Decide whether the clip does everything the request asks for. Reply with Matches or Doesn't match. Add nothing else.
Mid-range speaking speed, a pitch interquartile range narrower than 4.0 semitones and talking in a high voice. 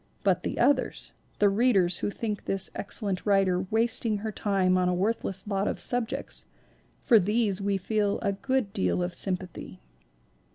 Matches